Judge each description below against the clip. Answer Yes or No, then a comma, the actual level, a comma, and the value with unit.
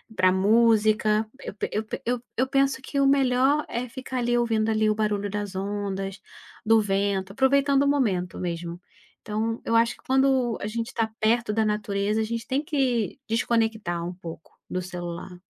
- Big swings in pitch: No, average, 3.7 semitones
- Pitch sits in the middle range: No, high, 220 Hz